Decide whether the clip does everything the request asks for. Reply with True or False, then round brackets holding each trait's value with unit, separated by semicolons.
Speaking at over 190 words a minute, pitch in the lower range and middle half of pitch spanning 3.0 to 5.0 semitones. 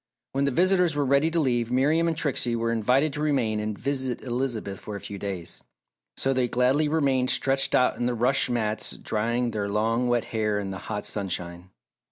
True (200 wpm; 125 Hz; 4.3 semitones)